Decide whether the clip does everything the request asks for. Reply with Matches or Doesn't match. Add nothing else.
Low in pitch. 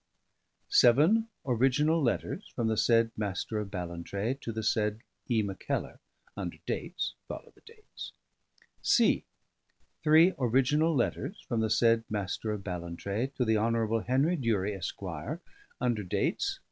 Matches